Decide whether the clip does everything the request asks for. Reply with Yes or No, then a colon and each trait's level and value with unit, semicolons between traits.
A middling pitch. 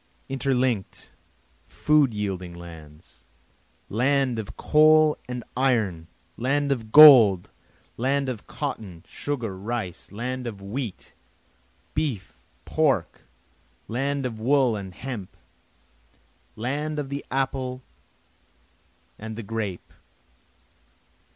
No: low, 120 Hz